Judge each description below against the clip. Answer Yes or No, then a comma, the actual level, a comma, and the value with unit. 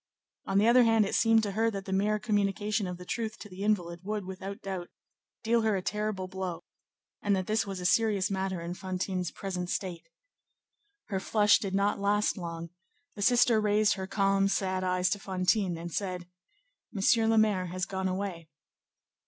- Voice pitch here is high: Yes, high, 195 Hz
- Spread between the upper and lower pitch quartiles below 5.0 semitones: Yes, narrow, 2.4 semitones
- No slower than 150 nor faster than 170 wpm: No, average, 185 wpm